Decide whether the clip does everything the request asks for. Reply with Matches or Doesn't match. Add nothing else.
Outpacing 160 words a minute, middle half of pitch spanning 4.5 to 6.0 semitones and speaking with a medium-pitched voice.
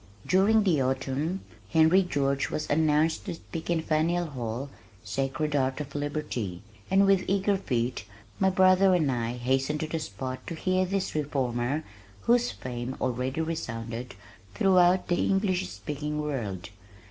Doesn't match